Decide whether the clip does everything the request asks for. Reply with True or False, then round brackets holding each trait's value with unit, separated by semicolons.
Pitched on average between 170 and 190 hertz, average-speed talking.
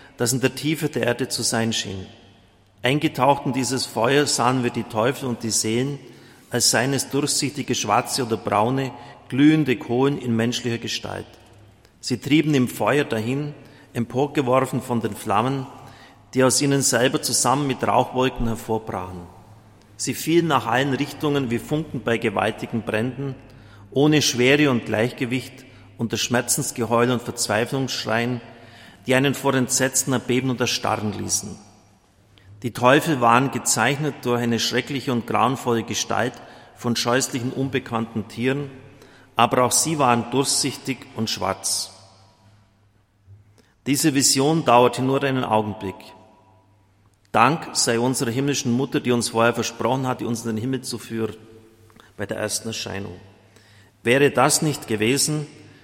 False (120 Hz; 135 wpm)